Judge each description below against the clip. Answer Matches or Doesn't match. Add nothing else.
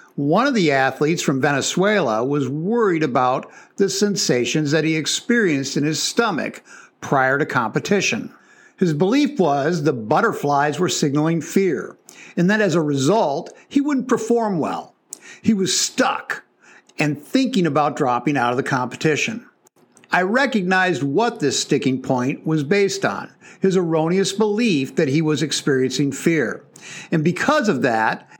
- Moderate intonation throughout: Doesn't match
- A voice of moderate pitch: Matches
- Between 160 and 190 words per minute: Doesn't match